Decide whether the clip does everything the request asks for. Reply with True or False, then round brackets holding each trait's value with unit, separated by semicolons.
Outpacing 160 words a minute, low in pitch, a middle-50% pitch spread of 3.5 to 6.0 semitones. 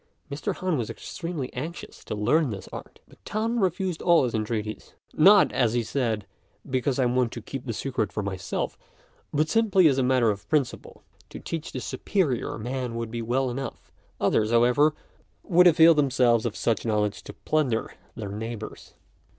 True (175 wpm; 130 Hz; 5.5 semitones)